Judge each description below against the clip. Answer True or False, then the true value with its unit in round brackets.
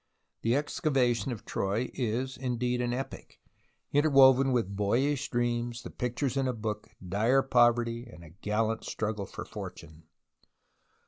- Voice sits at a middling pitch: False (120 Hz)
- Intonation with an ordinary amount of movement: True (3.0 semitones)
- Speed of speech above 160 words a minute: False (135 wpm)